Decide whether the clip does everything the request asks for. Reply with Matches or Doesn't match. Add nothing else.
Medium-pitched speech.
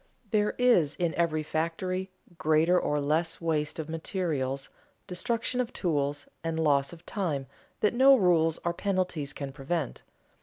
Matches